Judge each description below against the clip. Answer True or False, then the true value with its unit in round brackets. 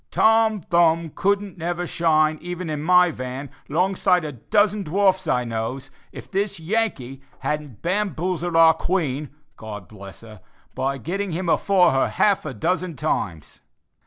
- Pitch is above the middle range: False (165 Hz)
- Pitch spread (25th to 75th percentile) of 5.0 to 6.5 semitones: True (5.4 semitones)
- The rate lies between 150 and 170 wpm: True (155 wpm)